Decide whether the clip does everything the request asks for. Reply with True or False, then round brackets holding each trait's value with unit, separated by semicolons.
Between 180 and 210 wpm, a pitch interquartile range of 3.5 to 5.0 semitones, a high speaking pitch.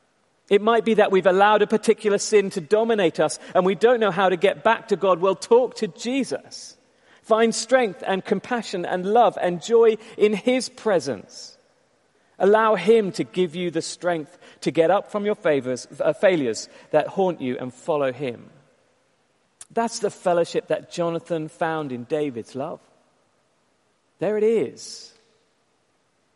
False (160 wpm; 4.5 semitones; 195 Hz)